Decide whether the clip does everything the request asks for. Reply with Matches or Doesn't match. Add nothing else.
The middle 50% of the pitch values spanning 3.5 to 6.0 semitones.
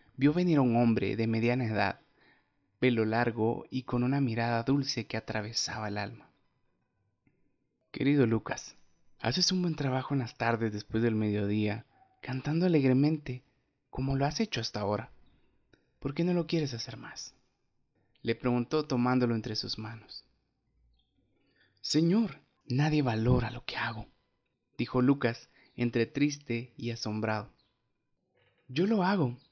Matches